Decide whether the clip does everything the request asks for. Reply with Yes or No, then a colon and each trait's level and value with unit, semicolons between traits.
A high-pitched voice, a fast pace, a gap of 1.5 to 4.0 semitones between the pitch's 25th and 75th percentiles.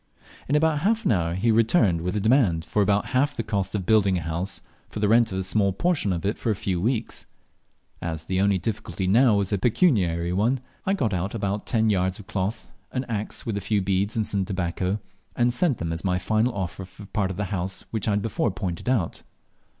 No: low, 100 Hz; fast, 235 wpm; average, 3.5 semitones